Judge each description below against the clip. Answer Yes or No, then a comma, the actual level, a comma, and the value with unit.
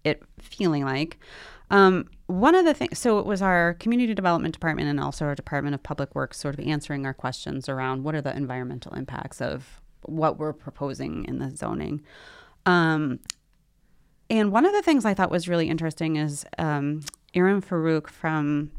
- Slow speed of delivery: No, average, 180 wpm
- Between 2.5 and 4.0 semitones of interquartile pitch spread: No, average, 4.4 semitones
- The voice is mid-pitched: Yes, medium, 160 Hz